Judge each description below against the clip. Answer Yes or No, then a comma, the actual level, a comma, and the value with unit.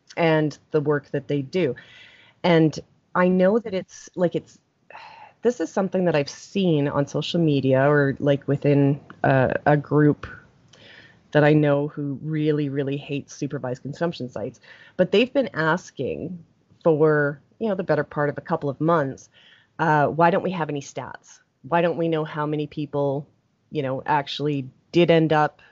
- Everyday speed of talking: Yes, average, 170 wpm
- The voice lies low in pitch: No, medium, 150 Hz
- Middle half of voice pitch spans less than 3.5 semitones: Yes, average, 3.0 semitones